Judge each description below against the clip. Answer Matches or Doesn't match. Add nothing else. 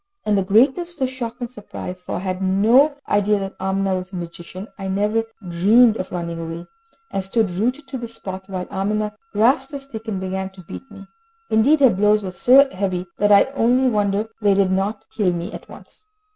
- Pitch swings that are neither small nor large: Matches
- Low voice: Doesn't match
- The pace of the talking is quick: Matches